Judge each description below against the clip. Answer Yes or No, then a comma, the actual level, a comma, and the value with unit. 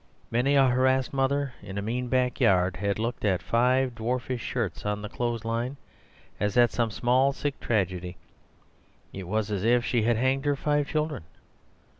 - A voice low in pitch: Yes, low, 120 Hz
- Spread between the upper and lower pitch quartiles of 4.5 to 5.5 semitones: No, average, 3.9 semitones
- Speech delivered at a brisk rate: No, average, 170 wpm